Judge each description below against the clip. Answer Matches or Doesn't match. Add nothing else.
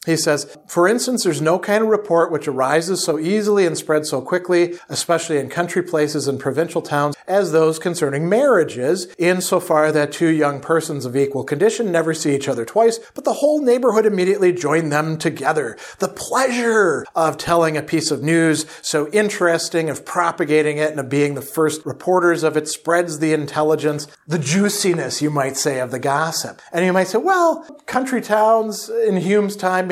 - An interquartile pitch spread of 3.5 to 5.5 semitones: Matches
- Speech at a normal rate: Matches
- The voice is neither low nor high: Matches